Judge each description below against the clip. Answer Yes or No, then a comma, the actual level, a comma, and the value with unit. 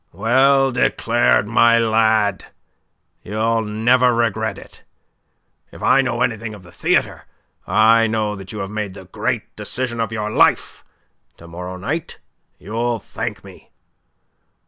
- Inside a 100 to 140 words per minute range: Yes, slow, 135 wpm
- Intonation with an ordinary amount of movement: No, narrow, 2.1 semitones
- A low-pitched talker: Yes, low, 110 Hz